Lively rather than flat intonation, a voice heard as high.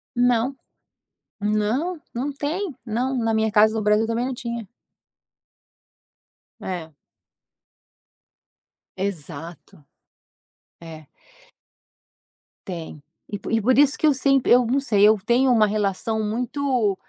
No: average, 4.0 semitones; high, 225 Hz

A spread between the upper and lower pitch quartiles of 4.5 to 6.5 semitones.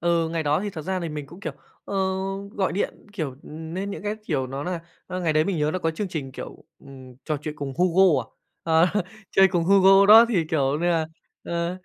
No: average, 3.7 semitones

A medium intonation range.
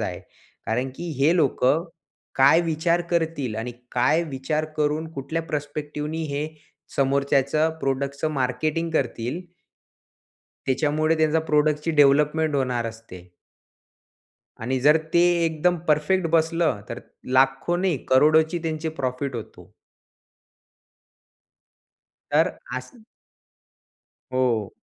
Yes: average, 3.3 semitones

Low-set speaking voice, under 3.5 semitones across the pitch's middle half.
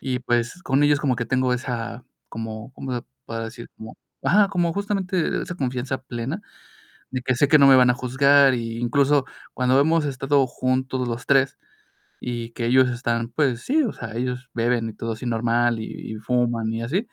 Yes: low, 125 Hz; average, 2.8 semitones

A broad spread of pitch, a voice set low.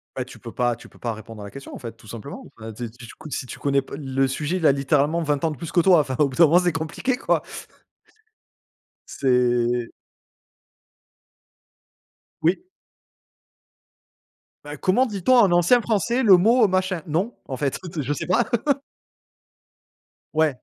No: wide, 6.0 semitones; medium, 150 Hz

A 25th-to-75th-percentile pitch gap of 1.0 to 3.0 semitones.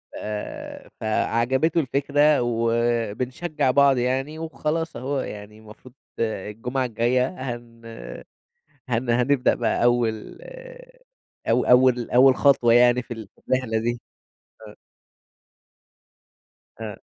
Yes: narrow, 2.4 semitones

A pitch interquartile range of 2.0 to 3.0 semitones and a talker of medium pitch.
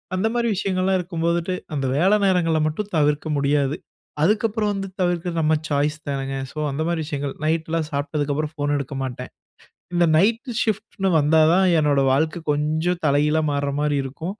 No: average, 4.1 semitones; medium, 160 Hz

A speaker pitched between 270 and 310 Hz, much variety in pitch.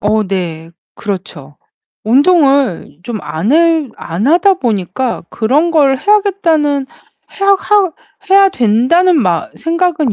Yes: very high, 275 Hz; wide, 8.4 semitones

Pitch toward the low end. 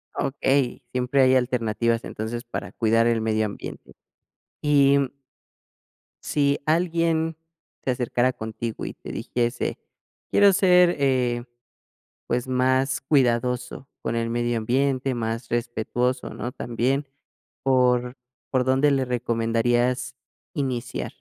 Yes: low, 125 Hz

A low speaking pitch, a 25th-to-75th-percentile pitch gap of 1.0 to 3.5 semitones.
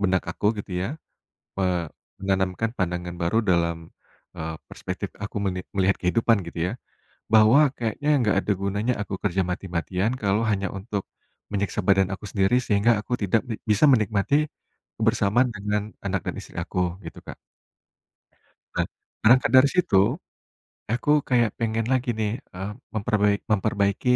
Yes: low, 100 Hz; average, 3.1 semitones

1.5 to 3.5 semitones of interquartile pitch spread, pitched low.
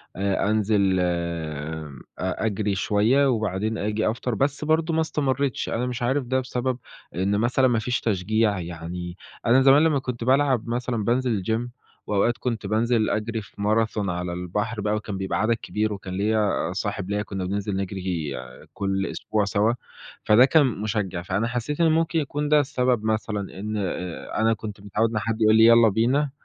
No: average, 3.9 semitones; low, 110 Hz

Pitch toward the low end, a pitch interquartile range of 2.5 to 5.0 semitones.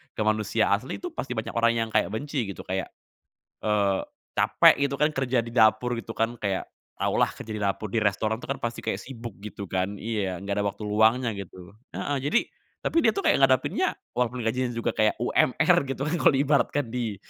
Yes: low, 115 Hz; average, 3.5 semitones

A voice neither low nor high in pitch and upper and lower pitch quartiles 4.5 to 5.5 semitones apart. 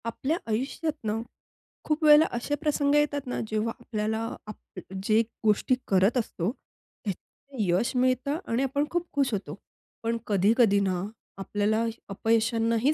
No: high, 230 Hz; average, 4.8 semitones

